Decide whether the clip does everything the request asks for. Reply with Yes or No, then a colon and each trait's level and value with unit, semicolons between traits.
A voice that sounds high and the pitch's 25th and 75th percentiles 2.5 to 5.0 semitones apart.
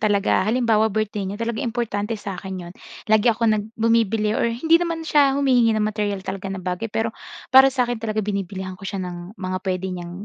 Yes: high, 215 Hz; average, 3.1 semitones